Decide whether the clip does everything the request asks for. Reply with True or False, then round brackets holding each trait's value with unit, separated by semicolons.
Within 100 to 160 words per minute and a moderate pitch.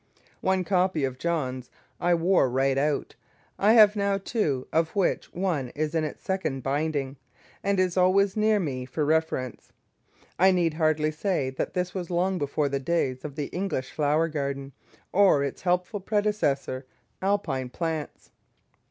True (155 wpm; 160 Hz)